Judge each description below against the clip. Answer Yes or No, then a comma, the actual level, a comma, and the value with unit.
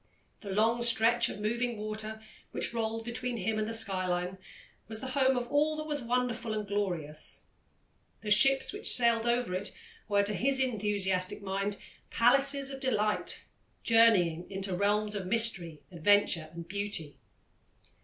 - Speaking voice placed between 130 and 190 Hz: No, high, 215 Hz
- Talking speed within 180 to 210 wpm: No, average, 150 wpm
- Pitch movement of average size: Yes, average, 3.4 semitones